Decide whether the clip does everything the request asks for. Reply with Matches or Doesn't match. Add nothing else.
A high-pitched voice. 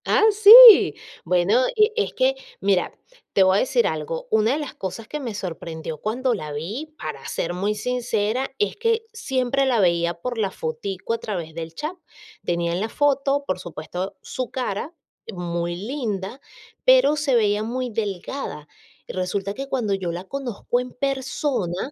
Matches